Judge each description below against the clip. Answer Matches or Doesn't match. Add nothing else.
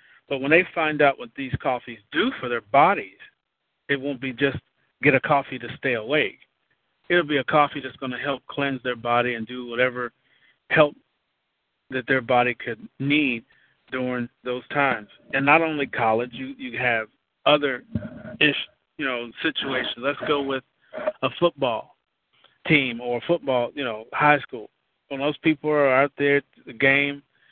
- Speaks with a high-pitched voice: Doesn't match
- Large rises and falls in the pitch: Doesn't match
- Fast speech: Doesn't match